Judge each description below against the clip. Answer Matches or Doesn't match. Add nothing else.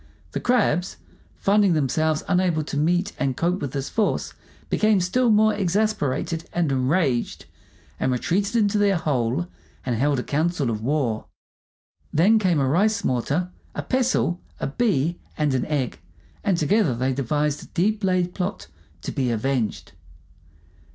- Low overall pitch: Doesn't match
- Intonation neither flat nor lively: Doesn't match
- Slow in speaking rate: Doesn't match